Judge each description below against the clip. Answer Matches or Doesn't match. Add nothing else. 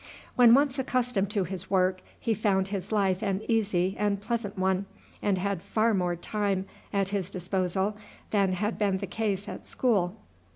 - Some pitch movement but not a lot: Doesn't match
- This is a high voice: Matches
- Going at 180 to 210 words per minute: Doesn't match